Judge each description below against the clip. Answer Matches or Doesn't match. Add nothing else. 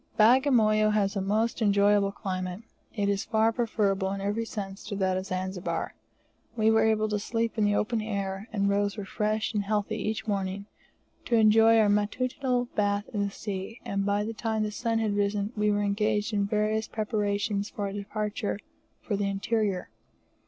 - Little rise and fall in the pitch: Matches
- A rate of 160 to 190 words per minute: Matches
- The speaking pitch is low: Doesn't match